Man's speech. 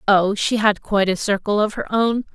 No: female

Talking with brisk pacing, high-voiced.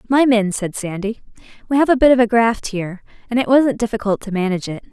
Yes: fast, 230 wpm; high, 225 Hz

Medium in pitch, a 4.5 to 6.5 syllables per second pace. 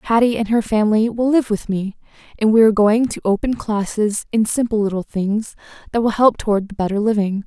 No: high, 215 Hz; 5.6 syllables/s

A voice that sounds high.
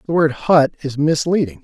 No: medium, 145 Hz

